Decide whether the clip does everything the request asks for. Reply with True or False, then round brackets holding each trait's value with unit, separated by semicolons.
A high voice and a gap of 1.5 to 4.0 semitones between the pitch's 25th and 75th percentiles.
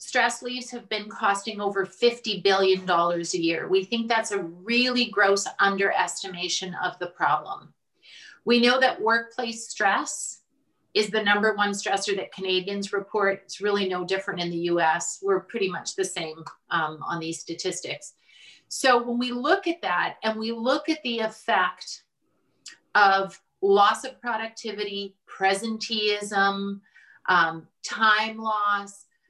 True (205 Hz; 3.2 semitones)